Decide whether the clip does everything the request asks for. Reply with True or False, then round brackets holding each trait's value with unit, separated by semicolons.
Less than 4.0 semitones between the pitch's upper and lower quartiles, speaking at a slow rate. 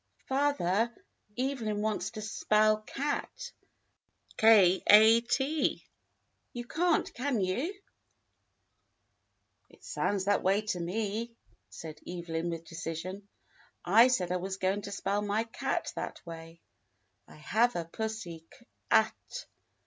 False (4.6 semitones; 125 wpm)